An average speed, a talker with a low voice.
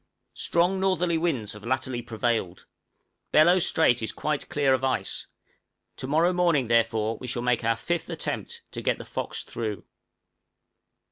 Yes: average, 150 wpm; low, 130 Hz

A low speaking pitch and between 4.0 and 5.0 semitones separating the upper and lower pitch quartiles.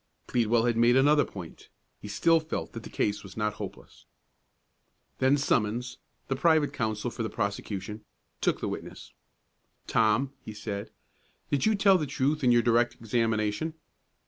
Yes: low, 120 Hz; average, 4.7 semitones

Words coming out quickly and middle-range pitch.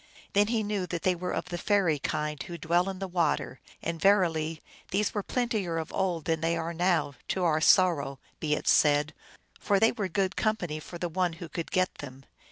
Yes: fast, 215 wpm; medium, 175 Hz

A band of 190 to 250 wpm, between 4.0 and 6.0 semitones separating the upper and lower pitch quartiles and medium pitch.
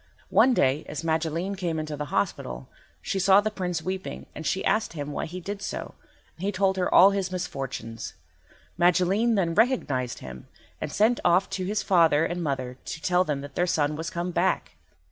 Yes: average, 195 wpm; average, 4.4 semitones; medium, 175 Hz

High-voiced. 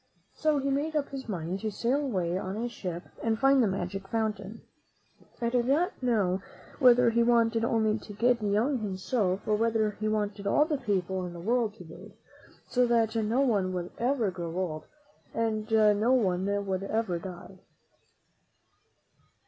Yes: high, 215 Hz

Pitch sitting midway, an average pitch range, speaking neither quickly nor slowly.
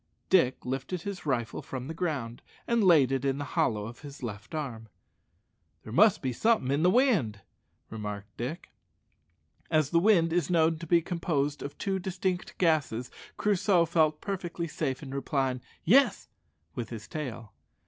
No: medium, 150 Hz; wide, 5.7 semitones; average, 160 wpm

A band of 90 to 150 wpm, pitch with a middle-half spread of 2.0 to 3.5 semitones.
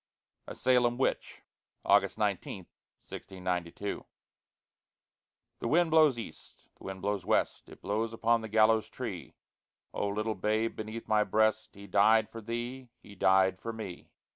Yes: average, 140 wpm; narrow, 2.5 semitones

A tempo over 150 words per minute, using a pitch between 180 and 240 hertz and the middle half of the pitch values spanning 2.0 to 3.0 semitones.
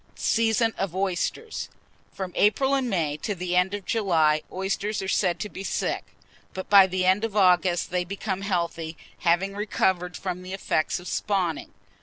Yes: average, 170 wpm; high, 190 Hz; narrow, 2.4 semitones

